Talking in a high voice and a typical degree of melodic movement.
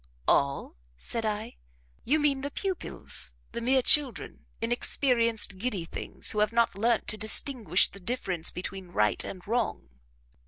Yes: high, 225 Hz; average, 4.5 semitones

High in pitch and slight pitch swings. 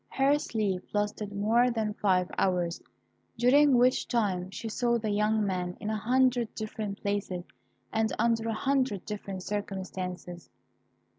No: high, 210 Hz; average, 3.5 semitones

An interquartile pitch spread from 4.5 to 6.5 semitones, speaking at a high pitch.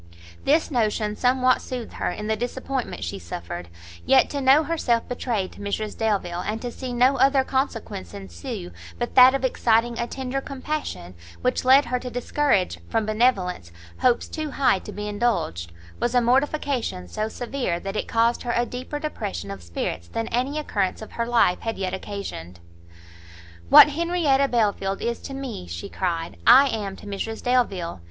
Yes: average, 5.1 semitones; high, 235 Hz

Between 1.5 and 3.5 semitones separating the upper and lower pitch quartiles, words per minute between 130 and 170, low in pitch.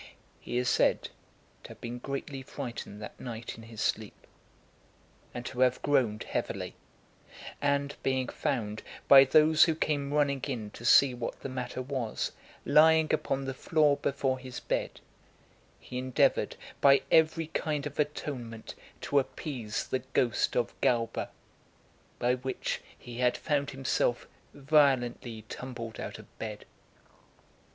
Yes: average, 2.9 semitones; average, 140 wpm; low, 130 Hz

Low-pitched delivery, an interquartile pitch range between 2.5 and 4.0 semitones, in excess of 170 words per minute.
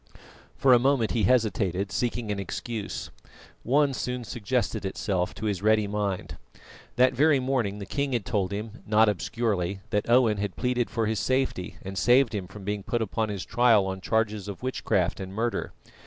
Yes: low, 110 Hz; average, 3.6 semitones; average, 180 wpm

